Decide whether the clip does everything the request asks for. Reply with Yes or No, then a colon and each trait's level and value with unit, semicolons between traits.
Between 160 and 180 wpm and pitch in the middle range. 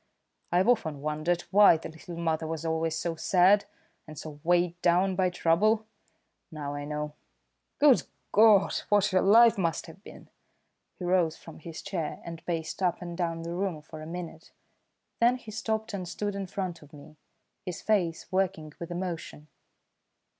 Yes: average, 170 wpm; medium, 175 Hz